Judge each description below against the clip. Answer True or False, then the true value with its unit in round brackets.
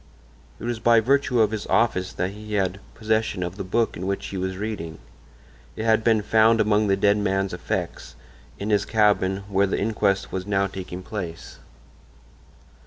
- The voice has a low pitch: True (100 Hz)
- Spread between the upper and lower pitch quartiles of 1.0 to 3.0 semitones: True (2.6 semitones)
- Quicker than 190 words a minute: False (175 wpm)